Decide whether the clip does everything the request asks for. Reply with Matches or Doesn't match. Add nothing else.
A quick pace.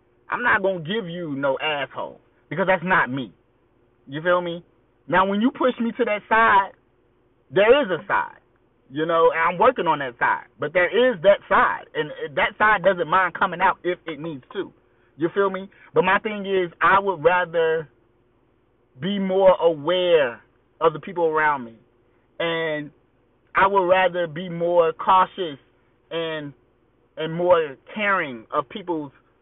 Doesn't match